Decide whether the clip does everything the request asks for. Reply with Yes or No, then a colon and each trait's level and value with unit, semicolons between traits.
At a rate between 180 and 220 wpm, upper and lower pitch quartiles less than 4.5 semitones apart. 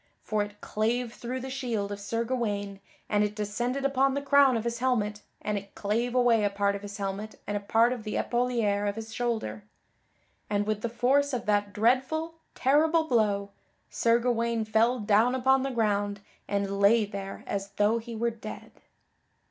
Yes: average, 185 wpm; average, 3.2 semitones